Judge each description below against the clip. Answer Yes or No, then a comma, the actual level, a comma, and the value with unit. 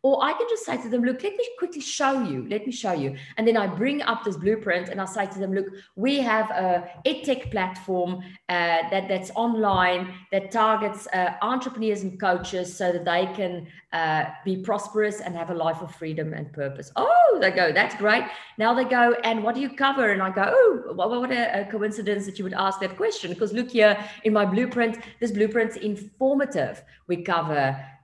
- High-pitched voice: Yes, high, 205 Hz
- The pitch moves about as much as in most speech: Yes, average, 4.4 semitones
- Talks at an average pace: No, fast, 210 wpm